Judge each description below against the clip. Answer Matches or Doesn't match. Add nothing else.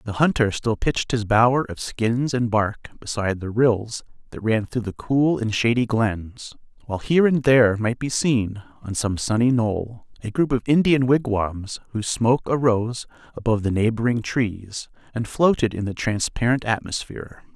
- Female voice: Doesn't match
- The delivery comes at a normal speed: Matches